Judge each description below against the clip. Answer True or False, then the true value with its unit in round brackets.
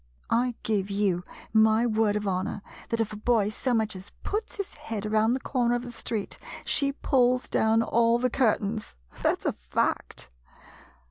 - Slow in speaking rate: False (180 wpm)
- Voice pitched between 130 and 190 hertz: False (225 Hz)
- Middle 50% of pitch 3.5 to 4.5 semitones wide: False (2.7 semitones)